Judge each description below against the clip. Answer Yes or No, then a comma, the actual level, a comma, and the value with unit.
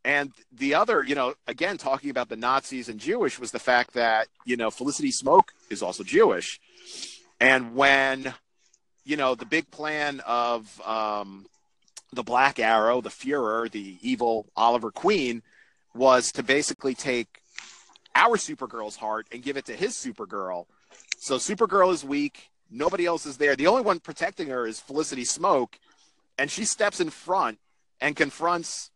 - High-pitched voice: No, low, 135 Hz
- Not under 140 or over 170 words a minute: Yes, average, 160 wpm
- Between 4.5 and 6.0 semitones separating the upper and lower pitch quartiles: Yes, average, 4.8 semitones